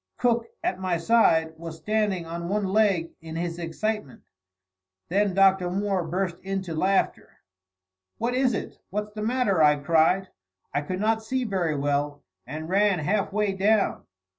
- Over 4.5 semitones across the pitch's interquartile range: No, average, 4.2 semitones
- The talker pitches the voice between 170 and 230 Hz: Yes, high, 190 Hz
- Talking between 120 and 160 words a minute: Yes, average, 155 wpm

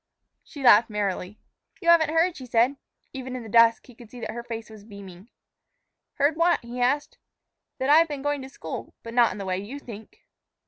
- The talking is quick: Yes, fast, 210 wpm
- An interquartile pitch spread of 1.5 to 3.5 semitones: No, average, 4.6 semitones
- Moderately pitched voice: No, high, 245 Hz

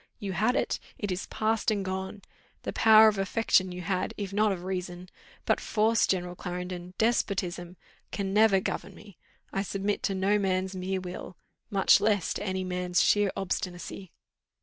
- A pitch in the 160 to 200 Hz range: Yes, high, 190 Hz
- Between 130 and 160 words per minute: No, average, 170 wpm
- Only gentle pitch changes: Yes, narrow, 2.2 semitones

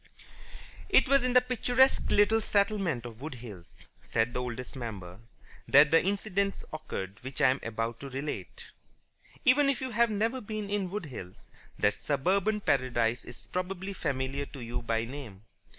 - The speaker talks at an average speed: Yes, average, 165 wpm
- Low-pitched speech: No, medium, 145 Hz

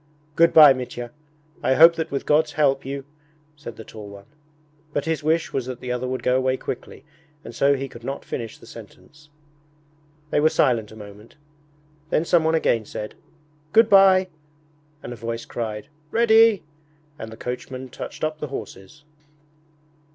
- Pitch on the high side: No, low, 135 Hz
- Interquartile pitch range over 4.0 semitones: Yes, average, 4.8 semitones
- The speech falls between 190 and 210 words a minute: No, average, 165 wpm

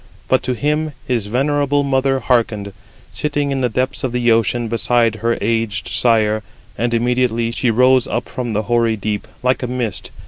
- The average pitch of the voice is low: Yes, low, 120 Hz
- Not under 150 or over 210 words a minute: Yes, average, 175 wpm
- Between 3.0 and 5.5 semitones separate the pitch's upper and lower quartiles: No, narrow, 2.4 semitones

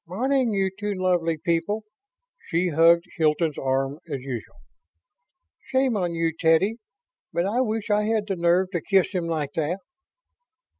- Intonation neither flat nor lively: Yes, average, 4.1 semitones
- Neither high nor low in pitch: Yes, medium, 175 Hz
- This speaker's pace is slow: No, average, 150 wpm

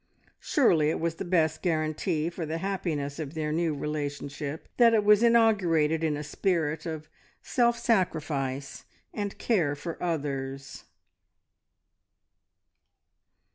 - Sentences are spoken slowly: Yes, slow, 120 wpm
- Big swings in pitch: No, average, 4.0 semitones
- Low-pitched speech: No, medium, 160 Hz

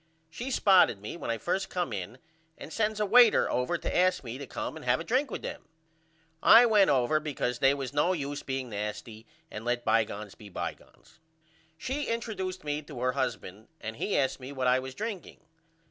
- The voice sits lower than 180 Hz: Yes, medium, 140 Hz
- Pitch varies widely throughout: Yes, wide, 7.7 semitones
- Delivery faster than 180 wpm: Yes, average, 200 wpm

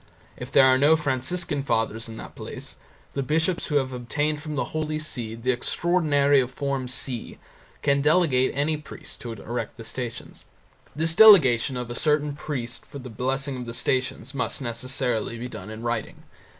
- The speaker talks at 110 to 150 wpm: No, average, 175 wpm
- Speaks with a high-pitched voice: No, low, 130 Hz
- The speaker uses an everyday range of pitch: Yes, average, 3.5 semitones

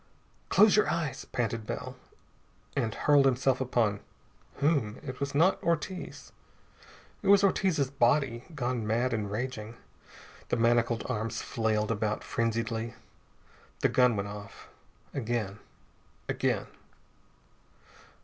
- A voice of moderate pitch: No, low, 120 Hz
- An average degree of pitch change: Yes, average, 3.9 semitones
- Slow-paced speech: Yes, slow, 110 wpm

